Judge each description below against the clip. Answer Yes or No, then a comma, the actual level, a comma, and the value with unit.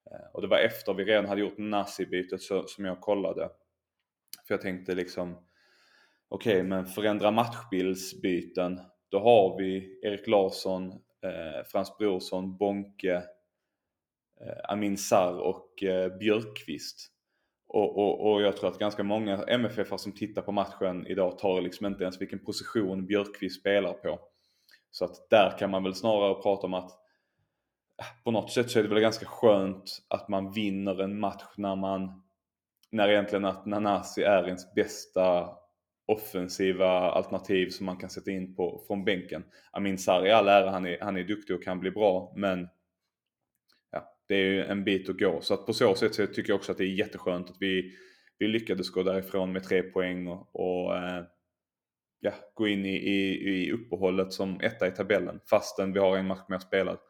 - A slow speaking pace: No, average, 175 wpm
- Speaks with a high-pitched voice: No, very low, 95 Hz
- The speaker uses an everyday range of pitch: No, narrow, 1.5 semitones